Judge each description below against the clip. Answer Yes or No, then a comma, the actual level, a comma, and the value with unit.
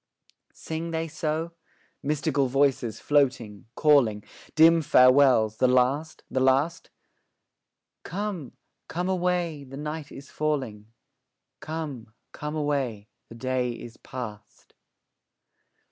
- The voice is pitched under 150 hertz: Yes, medium, 140 Hz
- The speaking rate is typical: No, slow, 100 wpm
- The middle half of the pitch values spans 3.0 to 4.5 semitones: Yes, average, 4.1 semitones